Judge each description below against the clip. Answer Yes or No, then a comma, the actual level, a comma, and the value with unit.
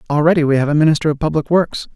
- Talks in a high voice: No, medium, 155 Hz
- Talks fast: Yes, fast, 245 wpm